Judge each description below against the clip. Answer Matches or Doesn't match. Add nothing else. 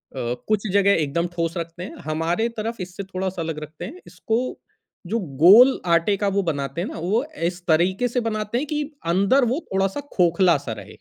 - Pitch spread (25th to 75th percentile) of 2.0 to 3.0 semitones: Doesn't match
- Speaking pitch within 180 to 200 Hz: Matches